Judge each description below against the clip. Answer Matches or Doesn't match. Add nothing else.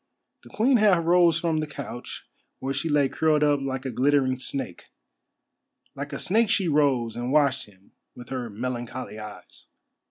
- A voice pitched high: Doesn't match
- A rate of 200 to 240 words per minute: Doesn't match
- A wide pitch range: Doesn't match